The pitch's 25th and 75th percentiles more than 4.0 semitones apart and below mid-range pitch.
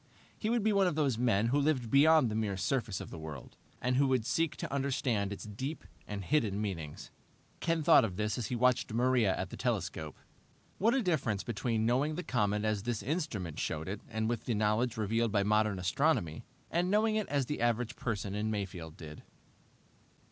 Yes: wide, 5.6 semitones; low, 115 Hz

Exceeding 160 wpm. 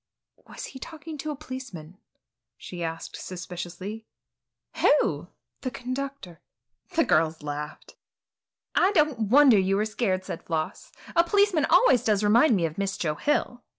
No: average, 145 wpm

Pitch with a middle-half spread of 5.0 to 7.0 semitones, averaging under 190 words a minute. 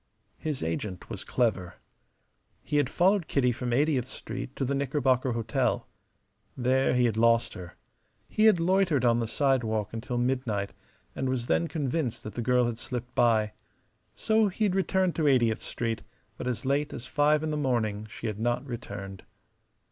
No: average, 4.2 semitones; average, 170 wpm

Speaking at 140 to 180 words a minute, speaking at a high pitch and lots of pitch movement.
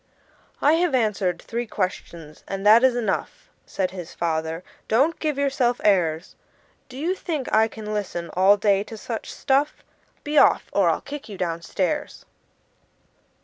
Yes: average, 155 wpm; high, 215 Hz; wide, 6.7 semitones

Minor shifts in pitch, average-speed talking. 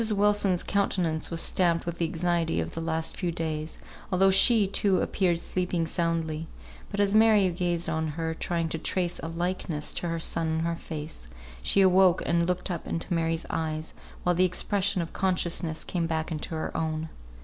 Yes: narrow, 2.2 semitones; average, 180 wpm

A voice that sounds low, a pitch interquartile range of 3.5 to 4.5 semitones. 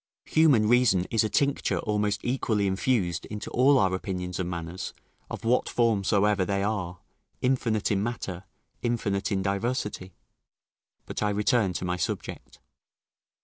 Yes: low, 105 Hz; average, 3.8 semitones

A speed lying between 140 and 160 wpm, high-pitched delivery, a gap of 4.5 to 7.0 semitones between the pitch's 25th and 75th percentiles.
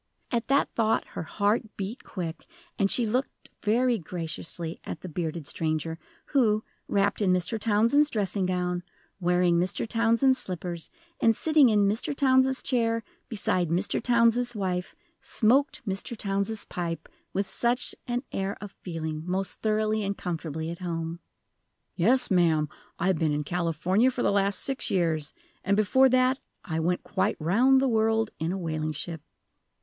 Yes: average, 155 wpm; high, 200 Hz; average, 5.1 semitones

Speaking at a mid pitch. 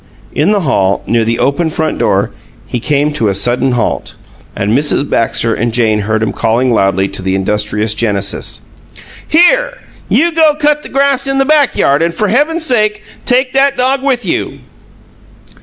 Yes: medium, 150 Hz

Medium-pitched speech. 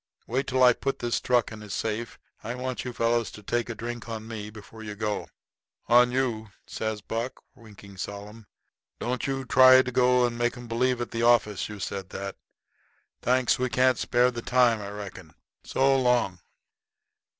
No: low, 120 Hz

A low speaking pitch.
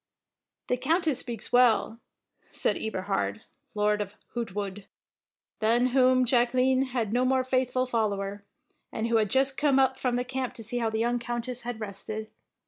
No: high, 240 Hz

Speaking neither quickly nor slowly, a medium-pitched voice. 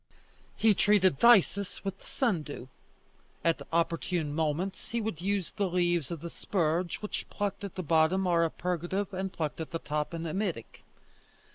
Yes: average, 165 wpm; medium, 175 Hz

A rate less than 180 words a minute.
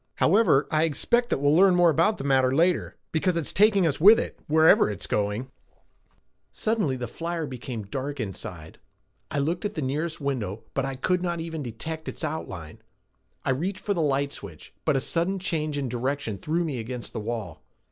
No: average, 190 wpm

